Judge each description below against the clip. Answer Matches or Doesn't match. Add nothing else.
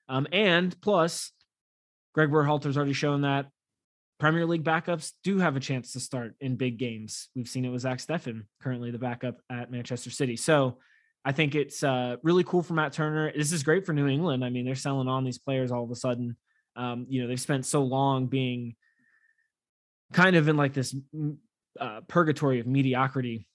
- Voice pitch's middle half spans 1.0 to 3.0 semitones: Doesn't match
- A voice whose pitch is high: Doesn't match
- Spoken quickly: Doesn't match